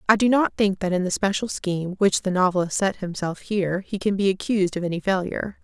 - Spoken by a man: No, female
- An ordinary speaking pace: No, fast, 235 wpm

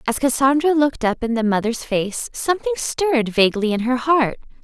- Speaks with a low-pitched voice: No, very high, 255 Hz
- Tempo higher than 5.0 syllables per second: Yes, 5.6 syllables/s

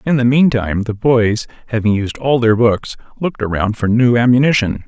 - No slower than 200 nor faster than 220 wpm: No, average, 185 wpm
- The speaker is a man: Yes, male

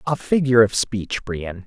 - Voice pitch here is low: Yes, low, 115 Hz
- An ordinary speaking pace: Yes, average, 180 wpm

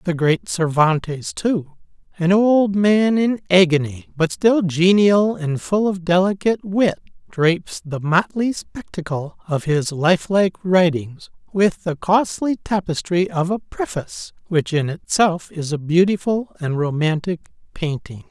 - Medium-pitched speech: Yes, medium, 175 Hz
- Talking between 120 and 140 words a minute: Yes, slow, 135 wpm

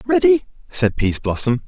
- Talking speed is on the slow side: Yes, slow, 110 wpm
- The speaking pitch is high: No, medium, 165 Hz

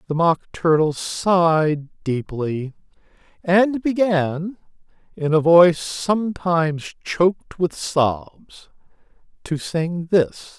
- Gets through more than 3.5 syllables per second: No, 3.1 syllables/s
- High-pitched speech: No, medium, 165 Hz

